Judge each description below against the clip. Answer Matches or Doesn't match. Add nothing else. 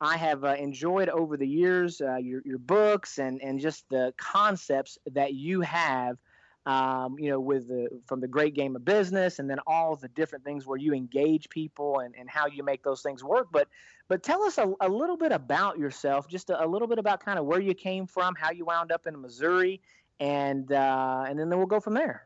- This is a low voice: Doesn't match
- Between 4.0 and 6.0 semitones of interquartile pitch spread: Matches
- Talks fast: Matches